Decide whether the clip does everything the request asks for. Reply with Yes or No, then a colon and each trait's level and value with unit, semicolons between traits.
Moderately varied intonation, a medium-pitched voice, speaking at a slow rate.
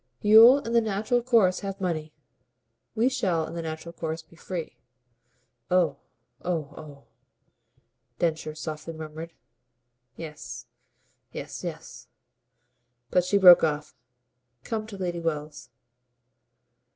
Yes: average, 4.0 semitones; medium, 170 Hz; slow, 115 wpm